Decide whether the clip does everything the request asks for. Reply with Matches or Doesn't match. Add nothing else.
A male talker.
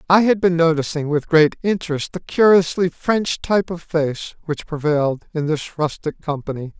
Matches